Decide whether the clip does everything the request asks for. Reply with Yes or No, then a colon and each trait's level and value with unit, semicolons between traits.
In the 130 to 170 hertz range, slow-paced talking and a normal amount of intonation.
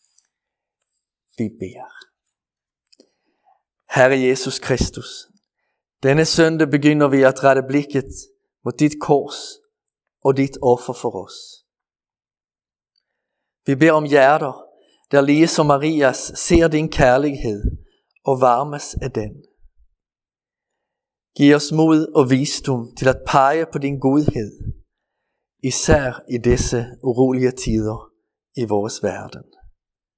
Yes: low, 135 Hz; slow, 105 wpm; average, 3.5 semitones